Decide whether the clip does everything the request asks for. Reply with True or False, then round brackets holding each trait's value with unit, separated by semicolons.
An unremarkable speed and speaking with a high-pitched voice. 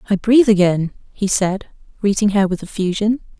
True (160 wpm; 200 Hz)